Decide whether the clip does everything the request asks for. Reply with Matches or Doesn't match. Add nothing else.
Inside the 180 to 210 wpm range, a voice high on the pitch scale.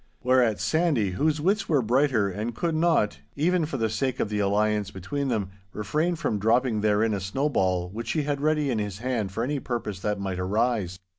Doesn't match